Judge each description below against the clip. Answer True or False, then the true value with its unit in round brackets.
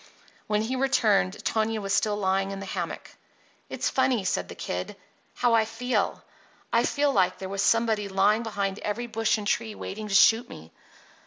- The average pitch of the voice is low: False (215 Hz)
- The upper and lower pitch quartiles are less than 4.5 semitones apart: True (2.7 semitones)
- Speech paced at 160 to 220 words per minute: True (180 wpm)